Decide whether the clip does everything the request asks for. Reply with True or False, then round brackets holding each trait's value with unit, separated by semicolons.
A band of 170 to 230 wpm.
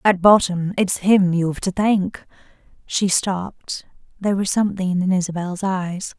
False (145 wpm)